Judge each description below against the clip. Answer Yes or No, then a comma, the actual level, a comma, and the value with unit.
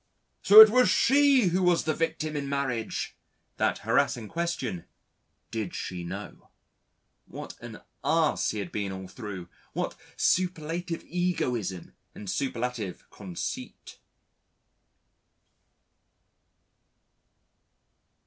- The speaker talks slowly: Yes, slow, 100 wpm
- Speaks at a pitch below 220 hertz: Yes, low, 135 Hz